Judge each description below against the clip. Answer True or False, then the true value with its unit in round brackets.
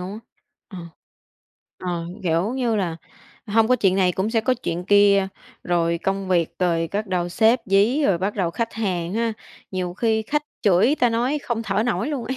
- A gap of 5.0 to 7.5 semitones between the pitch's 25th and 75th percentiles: False (4.2 semitones)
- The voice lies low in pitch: False (200 Hz)